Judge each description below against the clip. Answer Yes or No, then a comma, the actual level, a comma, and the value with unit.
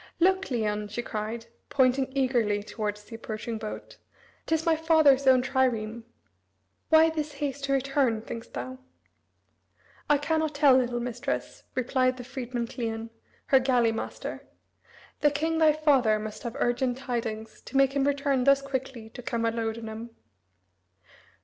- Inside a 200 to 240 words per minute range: No, average, 145 wpm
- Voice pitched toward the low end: No, very high, 255 Hz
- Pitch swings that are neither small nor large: Yes, average, 3.5 semitones